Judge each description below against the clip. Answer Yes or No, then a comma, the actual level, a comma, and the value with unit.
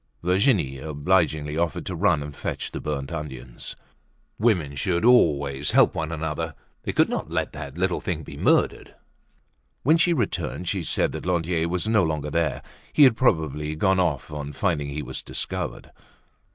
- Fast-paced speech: No, average, 165 wpm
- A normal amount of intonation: Yes, average, 4.0 semitones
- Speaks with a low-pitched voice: Yes, very low, 80 Hz